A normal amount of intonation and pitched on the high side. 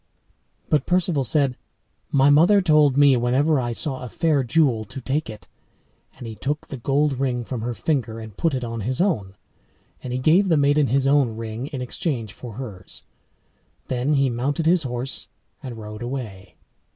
No: average, 3.7 semitones; low, 130 Hz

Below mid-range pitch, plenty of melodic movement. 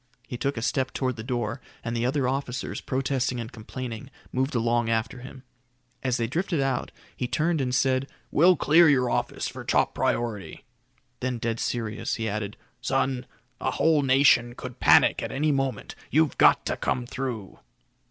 No: low, 130 Hz; narrow, 2.5 semitones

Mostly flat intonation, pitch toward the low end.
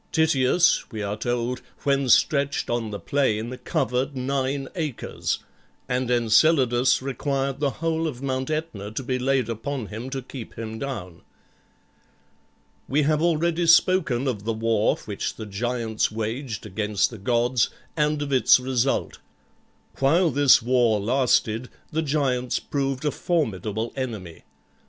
No: average, 3.8 semitones; low, 130 Hz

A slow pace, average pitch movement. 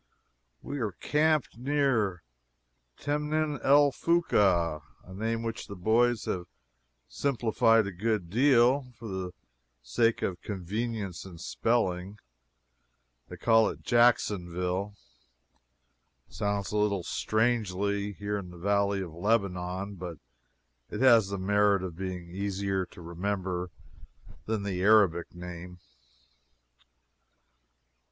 Yes: slow, 115 wpm; average, 4.0 semitones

